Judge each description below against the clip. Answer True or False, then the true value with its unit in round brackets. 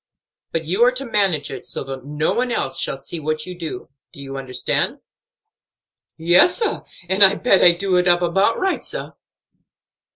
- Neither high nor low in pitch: True (175 Hz)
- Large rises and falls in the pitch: False (4.6 semitones)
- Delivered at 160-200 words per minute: True (185 wpm)